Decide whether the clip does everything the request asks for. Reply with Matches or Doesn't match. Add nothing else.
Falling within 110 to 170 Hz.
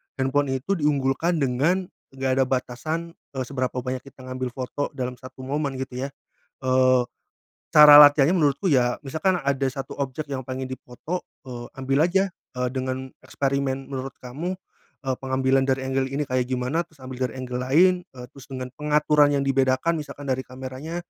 Matches